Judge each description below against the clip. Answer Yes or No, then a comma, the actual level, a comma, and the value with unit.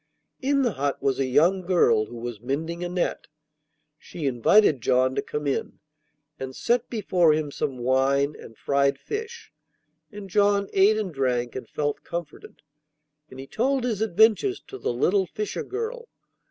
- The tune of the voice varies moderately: No, wide, 8.1 semitones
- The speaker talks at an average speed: Yes, average, 165 wpm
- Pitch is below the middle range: No, medium, 170 Hz